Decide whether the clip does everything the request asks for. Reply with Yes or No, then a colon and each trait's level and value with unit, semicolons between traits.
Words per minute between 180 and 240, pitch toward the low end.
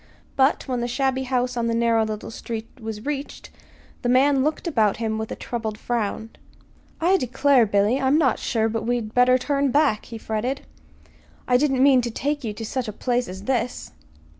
No: average, 190 wpm; high, 245 Hz